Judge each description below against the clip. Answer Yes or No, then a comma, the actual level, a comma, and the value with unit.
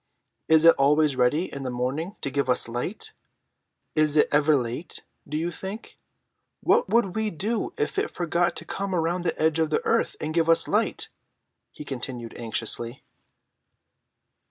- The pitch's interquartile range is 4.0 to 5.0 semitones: Yes, average, 4.7 semitones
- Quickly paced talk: No, average, 165 wpm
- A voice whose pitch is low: No, medium, 155 Hz